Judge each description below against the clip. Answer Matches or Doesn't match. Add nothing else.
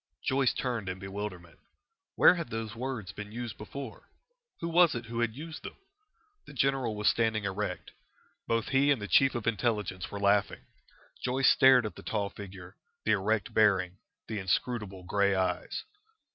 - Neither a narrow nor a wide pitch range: Matches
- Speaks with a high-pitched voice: Doesn't match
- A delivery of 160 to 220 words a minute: Matches